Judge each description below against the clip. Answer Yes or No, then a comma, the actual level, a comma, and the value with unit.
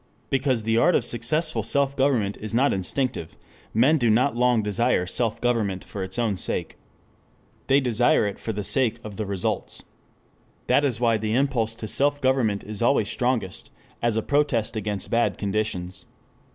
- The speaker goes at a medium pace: Yes, average, 170 wpm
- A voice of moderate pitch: No, low, 115 Hz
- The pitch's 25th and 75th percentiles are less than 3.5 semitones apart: No, average, 3.8 semitones